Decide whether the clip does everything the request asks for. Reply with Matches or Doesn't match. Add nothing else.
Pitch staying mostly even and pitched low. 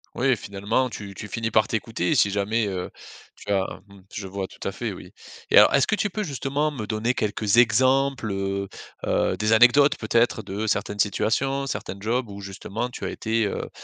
Doesn't match